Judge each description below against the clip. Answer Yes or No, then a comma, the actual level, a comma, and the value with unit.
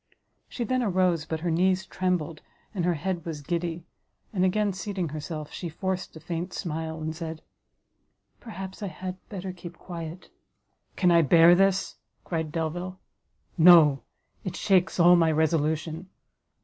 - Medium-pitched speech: Yes, medium, 175 Hz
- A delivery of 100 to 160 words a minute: Yes, average, 150 wpm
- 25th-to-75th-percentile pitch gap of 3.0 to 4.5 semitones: No, narrow, 2.6 semitones